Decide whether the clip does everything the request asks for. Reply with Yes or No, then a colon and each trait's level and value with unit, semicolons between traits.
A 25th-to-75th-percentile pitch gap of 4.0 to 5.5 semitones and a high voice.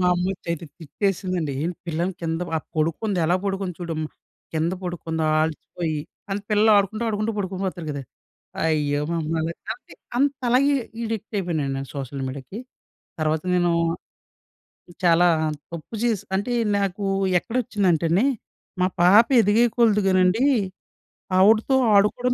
No: average, 4.6 semitones; medium, 180 Hz